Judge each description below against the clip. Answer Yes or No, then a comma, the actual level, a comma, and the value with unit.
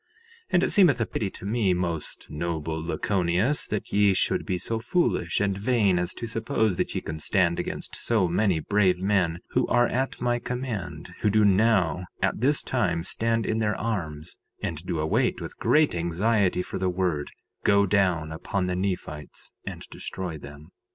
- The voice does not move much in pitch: No, average, 4.5 semitones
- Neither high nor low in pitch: No, very low, 95 Hz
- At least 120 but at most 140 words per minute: No, average, 180 wpm